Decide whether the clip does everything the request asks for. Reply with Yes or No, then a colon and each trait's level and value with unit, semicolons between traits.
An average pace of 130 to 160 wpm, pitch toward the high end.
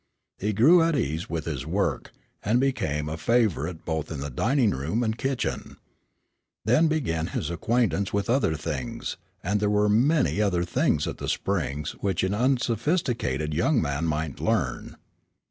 No: average, 155 wpm; low, 100 Hz